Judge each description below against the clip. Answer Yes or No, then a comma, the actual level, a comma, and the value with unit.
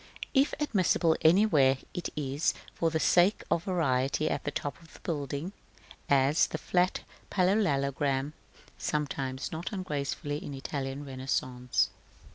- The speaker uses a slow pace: Yes, slow, 125 wpm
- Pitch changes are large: No, average, 4.4 semitones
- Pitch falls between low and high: Yes, medium, 150 Hz